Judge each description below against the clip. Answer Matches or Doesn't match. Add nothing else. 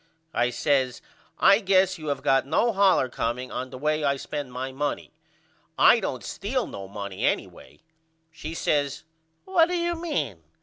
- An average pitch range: Doesn't match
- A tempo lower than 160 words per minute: Doesn't match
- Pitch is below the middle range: Doesn't match